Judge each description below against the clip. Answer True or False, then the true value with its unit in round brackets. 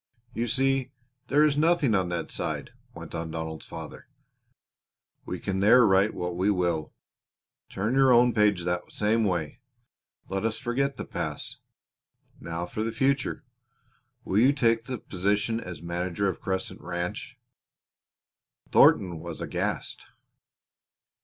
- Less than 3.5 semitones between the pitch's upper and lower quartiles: False (5.5 semitones)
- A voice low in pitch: True (105 Hz)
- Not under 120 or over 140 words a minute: True (135 wpm)